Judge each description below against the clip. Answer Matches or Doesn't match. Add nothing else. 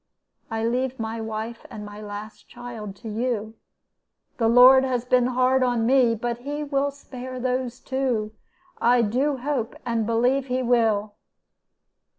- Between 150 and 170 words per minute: Matches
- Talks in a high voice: Matches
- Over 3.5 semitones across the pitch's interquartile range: Doesn't match